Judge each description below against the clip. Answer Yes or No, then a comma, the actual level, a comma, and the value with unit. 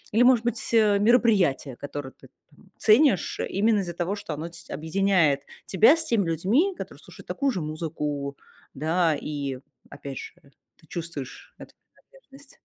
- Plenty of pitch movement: Yes, wide, 7.0 semitones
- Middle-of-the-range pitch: Yes, medium, 180 Hz